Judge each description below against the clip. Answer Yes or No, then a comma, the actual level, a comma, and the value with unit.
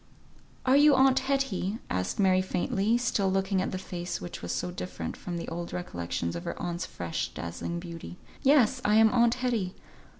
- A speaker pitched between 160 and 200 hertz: Yes, high, 190 Hz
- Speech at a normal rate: Yes, average, 180 wpm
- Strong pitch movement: Yes, wide, 6.0 semitones